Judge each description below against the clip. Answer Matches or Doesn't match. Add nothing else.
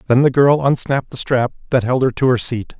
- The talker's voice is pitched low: Matches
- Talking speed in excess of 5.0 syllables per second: Matches